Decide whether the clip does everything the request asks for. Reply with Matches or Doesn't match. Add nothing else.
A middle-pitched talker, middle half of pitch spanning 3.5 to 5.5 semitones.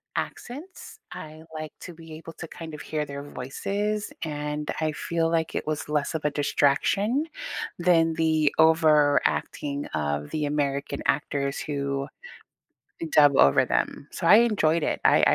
Doesn't match